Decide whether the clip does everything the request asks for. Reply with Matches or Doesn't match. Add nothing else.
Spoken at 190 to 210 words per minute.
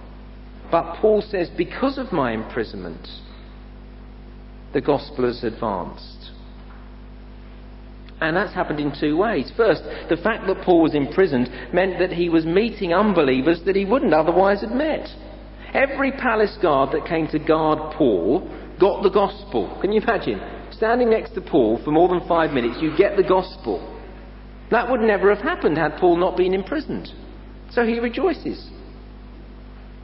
Doesn't match